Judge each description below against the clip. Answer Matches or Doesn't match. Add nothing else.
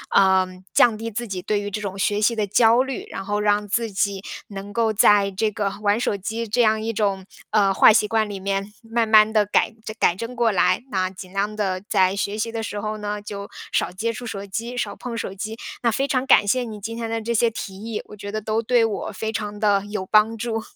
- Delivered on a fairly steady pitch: Matches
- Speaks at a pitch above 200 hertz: Matches